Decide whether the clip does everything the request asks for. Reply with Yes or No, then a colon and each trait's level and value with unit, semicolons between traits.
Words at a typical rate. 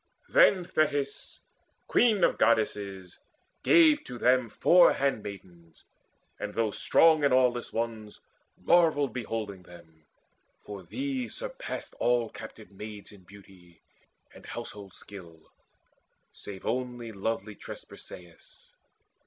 No: slow, 110 wpm